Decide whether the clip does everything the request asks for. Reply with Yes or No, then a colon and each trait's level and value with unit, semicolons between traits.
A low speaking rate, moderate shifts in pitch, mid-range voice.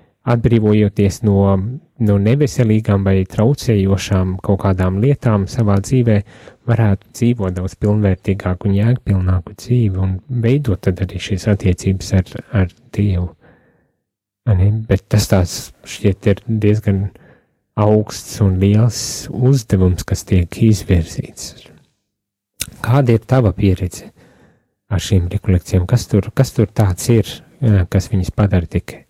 No: slow, 105 wpm; average, 3.2 semitones; low, 100 Hz